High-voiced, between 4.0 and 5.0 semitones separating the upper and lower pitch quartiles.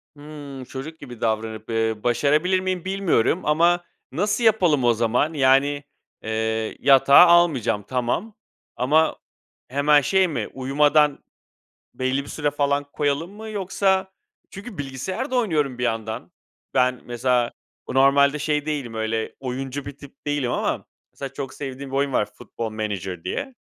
No: medium, 140 Hz; average, 4.4 semitones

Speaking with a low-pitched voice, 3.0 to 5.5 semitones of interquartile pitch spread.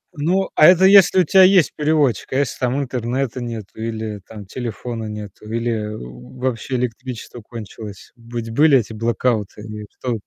Yes: low, 120 Hz; average, 3.8 semitones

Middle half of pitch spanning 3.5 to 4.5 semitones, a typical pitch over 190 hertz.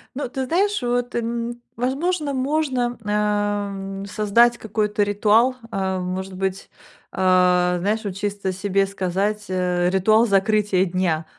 Yes: average, 4.2 semitones; high, 205 Hz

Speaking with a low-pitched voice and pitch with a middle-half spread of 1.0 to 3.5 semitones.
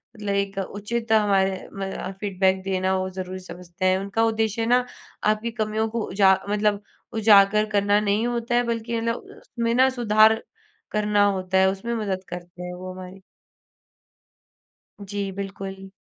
No: high, 200 Hz; narrow, 2.5 semitones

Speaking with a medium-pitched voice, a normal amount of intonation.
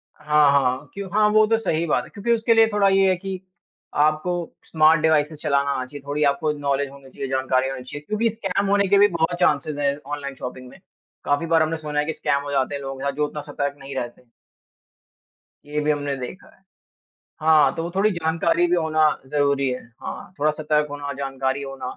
Yes: medium, 150 Hz; average, 3.3 semitones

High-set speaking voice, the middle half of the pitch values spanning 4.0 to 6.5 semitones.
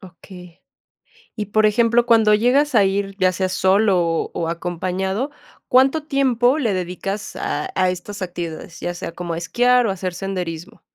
Yes: high, 195 Hz; average, 4.5 semitones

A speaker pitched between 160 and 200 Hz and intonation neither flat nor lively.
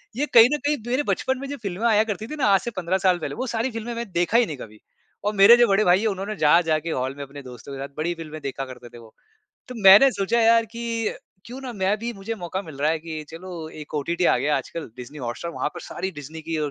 No: medium, 185 Hz; wide, 6.7 semitones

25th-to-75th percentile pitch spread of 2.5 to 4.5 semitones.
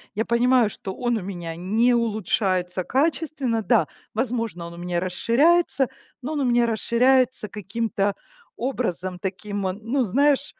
No: average, 4.9 semitones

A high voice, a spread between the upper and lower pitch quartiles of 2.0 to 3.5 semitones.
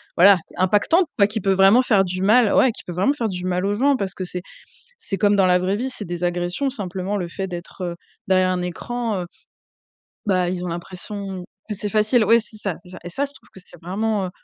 Yes: high, 195 Hz; average, 3.0 semitones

